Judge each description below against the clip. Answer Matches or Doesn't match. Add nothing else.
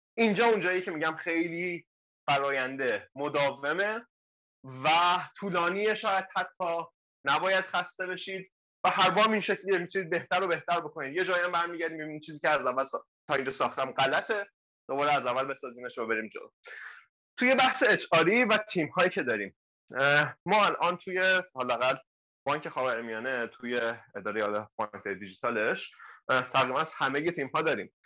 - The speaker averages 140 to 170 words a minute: Matches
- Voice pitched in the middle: Matches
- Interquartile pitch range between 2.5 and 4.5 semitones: Doesn't match